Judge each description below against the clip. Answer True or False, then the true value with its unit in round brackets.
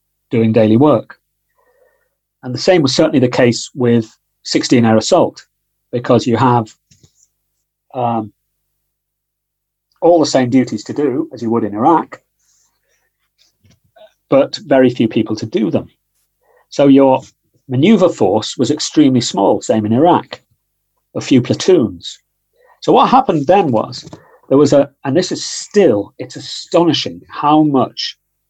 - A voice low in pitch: True (130 Hz)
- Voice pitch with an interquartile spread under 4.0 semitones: False (5.1 semitones)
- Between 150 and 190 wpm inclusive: False (135 wpm)